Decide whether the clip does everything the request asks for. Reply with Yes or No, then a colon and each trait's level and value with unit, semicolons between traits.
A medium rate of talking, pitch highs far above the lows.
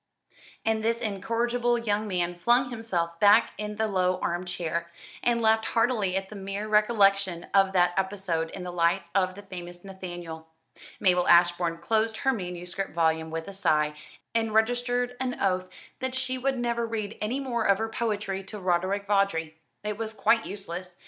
No: average, 170 wpm; average, 4.1 semitones